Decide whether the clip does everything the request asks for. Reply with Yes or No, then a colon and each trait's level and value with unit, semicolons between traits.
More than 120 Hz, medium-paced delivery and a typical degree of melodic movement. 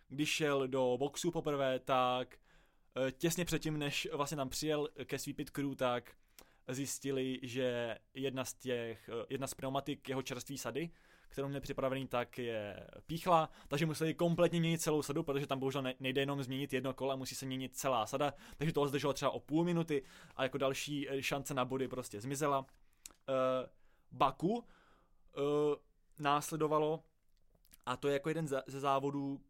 No: medium, 140 Hz; average, 155 wpm; narrow, 2.2 semitones